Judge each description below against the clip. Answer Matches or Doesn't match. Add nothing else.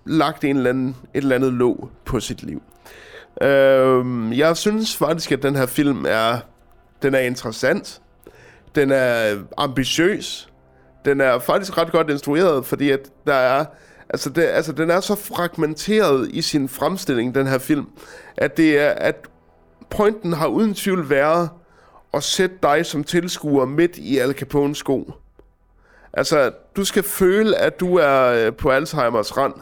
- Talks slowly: Doesn't match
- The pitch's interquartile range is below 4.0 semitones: Doesn't match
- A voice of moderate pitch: Matches